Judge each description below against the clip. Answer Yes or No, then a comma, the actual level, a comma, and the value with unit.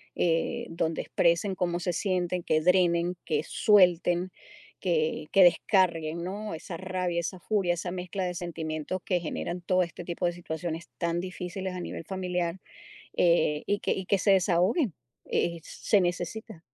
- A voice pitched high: No, medium, 175 Hz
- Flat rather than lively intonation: Yes, narrow, 1.6 semitones